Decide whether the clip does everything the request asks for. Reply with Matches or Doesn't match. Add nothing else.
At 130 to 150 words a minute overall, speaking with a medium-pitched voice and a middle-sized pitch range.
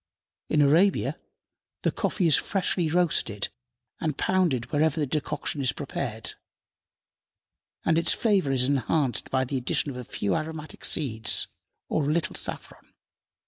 Matches